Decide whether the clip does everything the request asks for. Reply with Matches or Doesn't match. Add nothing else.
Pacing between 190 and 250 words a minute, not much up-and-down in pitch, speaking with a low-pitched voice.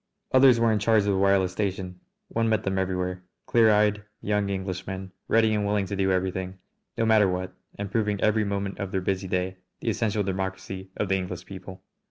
Matches